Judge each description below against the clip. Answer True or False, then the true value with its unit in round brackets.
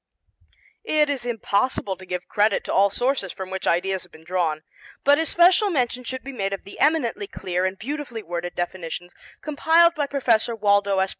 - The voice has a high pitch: True (205 Hz)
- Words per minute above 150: True (180 wpm)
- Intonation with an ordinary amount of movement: False (6.7 semitones)